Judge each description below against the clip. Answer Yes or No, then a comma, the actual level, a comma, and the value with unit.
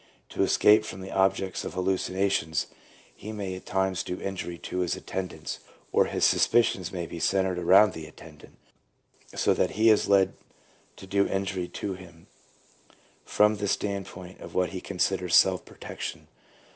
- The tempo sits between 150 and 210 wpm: Yes, average, 160 wpm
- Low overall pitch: Yes, very low, 95 Hz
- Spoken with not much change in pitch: Yes, narrow, 1.5 semitones